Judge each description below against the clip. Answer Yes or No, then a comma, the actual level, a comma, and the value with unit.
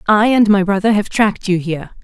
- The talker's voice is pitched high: Yes, high, 200 Hz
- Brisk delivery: Yes, fast, 235 wpm